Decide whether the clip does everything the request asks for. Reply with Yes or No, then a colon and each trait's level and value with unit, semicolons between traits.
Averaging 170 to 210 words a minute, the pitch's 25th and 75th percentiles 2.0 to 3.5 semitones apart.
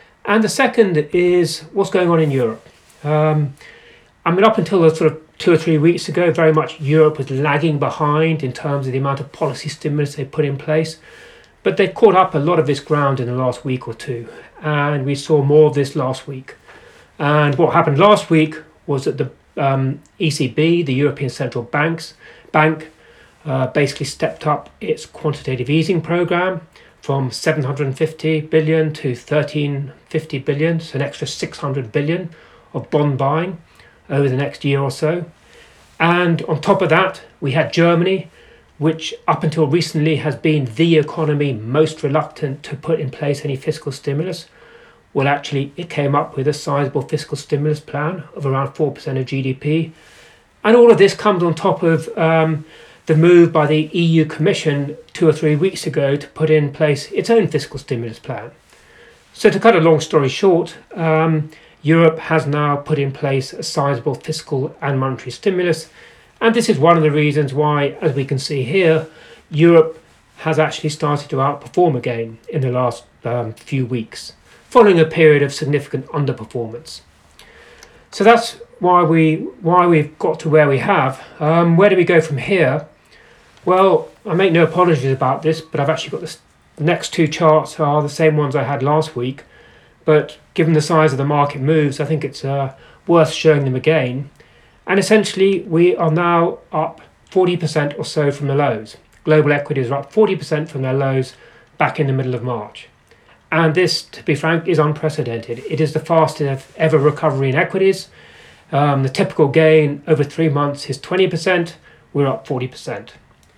Yes: average, 180 wpm; narrow, 2.6 semitones